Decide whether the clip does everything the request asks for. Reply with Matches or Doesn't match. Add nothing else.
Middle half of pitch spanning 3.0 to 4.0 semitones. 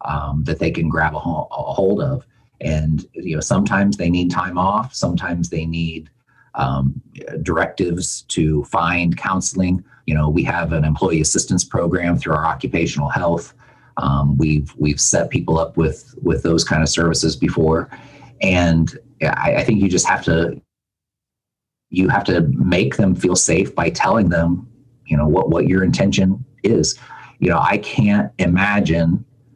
Matches